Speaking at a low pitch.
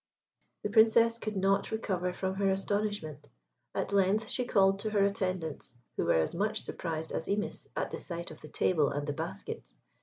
No: high, 195 Hz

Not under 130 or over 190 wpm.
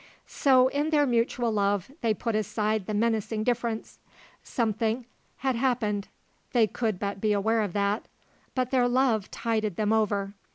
Yes: average, 155 wpm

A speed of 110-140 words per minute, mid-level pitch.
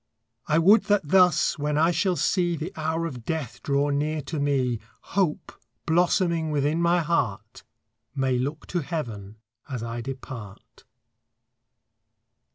Yes: slow, 135 wpm; medium, 150 Hz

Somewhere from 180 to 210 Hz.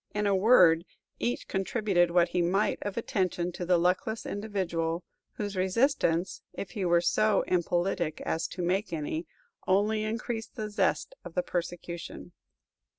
Yes: medium, 185 Hz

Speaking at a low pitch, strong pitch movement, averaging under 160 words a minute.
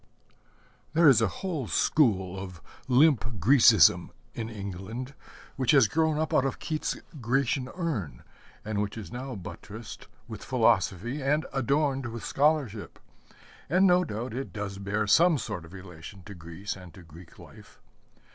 Yes: low, 115 Hz; wide, 6.0 semitones; average, 150 wpm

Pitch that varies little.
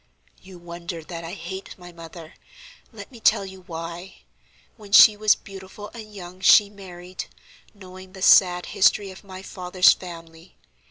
Yes: narrow, 2.2 semitones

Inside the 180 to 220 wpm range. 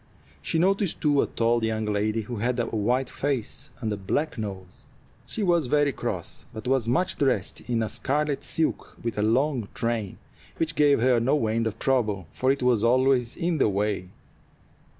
Yes: average, 185 wpm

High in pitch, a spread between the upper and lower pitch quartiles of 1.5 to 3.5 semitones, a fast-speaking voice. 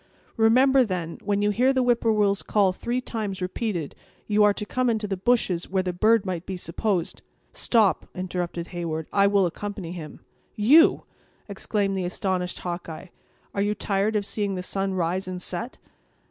No: high, 200 Hz; average, 3.1 semitones; average, 175 wpm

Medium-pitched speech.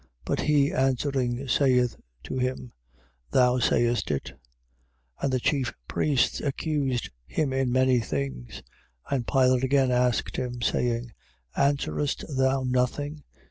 No: low, 130 Hz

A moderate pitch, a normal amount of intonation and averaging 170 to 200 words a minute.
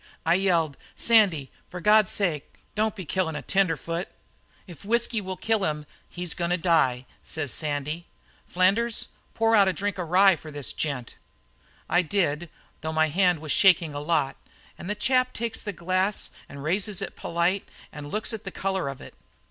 Yes: medium, 180 Hz; average, 4.2 semitones; average, 180 wpm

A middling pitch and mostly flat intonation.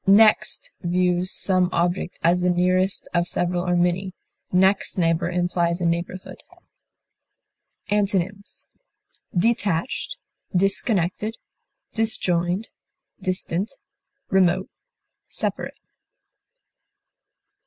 Yes: medium, 180 Hz; narrow, 2.0 semitones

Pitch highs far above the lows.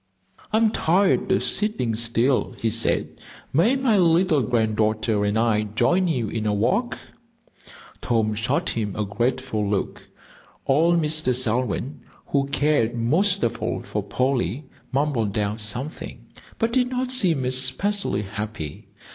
Yes: wide, 7.6 semitones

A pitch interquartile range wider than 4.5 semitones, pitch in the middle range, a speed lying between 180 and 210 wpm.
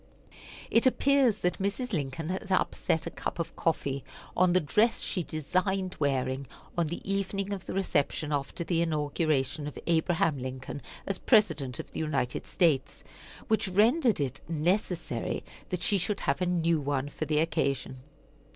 No: average, 5.1 semitones; medium, 165 Hz; average, 160 wpm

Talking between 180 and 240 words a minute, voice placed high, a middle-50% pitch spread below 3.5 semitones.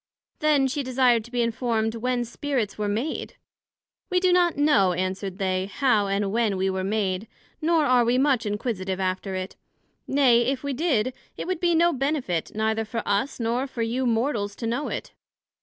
No: average, 185 wpm; high, 235 Hz; average, 4.9 semitones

